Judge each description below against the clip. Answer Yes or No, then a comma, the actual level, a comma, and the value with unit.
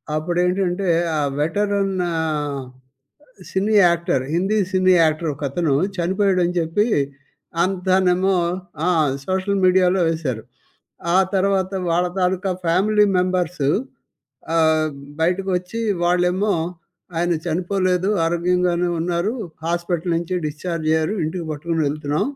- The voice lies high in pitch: No, medium, 180 Hz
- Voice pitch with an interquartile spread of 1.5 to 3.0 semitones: Yes, narrow, 2.4 semitones